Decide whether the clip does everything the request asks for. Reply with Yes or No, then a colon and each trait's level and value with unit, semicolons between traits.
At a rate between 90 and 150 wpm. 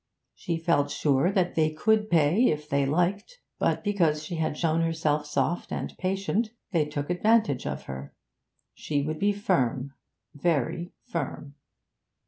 Yes: average, 145 wpm